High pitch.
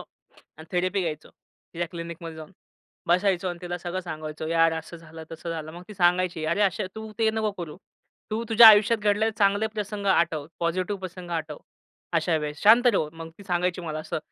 No: medium, 175 Hz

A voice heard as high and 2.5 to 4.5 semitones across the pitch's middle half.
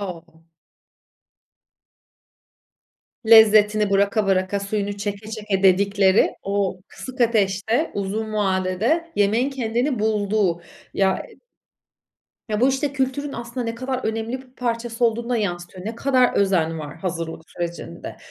Yes: high, 210 Hz; average, 3.6 semitones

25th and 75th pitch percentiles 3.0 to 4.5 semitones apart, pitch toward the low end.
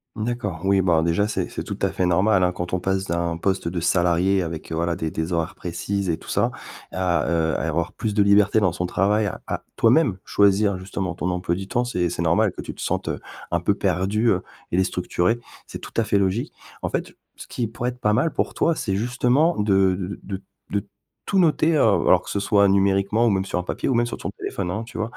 Yes: average, 3.4 semitones; very low, 95 Hz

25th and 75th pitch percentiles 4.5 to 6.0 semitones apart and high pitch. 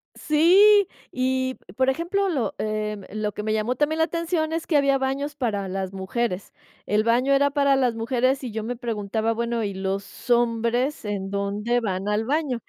Yes: average, 4.8 semitones; high, 240 Hz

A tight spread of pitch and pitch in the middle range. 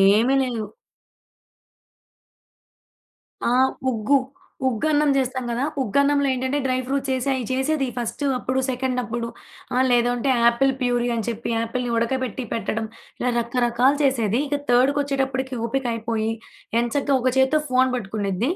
No: narrow, 2.3 semitones; very high, 255 Hz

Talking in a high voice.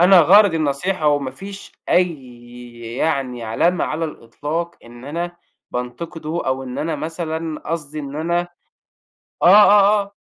No: medium, 155 Hz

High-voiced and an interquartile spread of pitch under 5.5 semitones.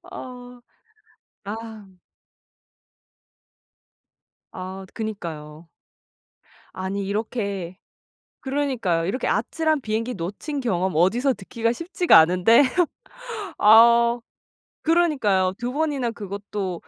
Yes: high, 215 Hz; average, 5.1 semitones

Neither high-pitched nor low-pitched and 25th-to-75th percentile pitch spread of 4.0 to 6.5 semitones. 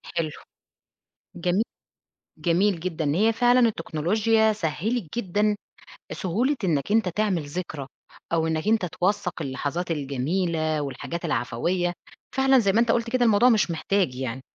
Yes: medium, 180 Hz; wide, 5.5 semitones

